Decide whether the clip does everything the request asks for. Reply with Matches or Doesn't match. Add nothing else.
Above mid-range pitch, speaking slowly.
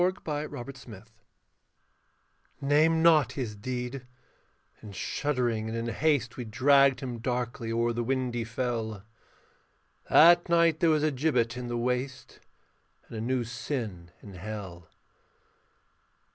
Doesn't match